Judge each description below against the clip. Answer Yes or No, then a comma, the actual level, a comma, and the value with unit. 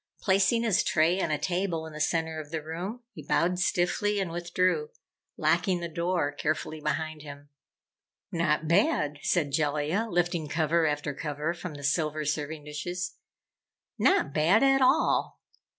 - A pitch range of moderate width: Yes, average, 3.1 semitones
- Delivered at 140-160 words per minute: Yes, average, 150 wpm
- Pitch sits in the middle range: Yes, medium, 165 Hz